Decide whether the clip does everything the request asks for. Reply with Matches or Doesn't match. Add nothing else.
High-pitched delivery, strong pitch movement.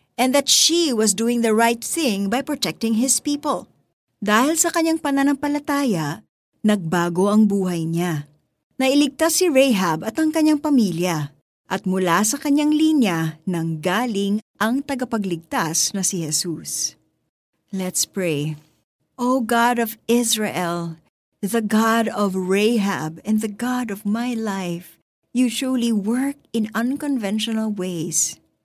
Matches